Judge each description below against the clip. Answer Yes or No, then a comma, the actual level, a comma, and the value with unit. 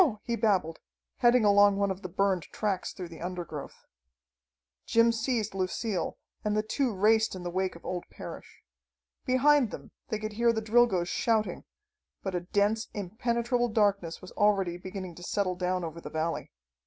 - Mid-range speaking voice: No, high, 200 Hz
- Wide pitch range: No, average, 3.6 semitones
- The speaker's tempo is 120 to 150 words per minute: No, average, 165 wpm